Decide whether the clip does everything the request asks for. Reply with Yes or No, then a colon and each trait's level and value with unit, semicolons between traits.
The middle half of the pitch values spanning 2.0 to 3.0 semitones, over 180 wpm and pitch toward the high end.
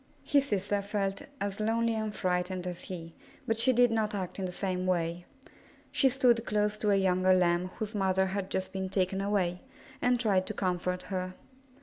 Yes: narrow, 2.6 semitones; average, 190 wpm; high, 195 Hz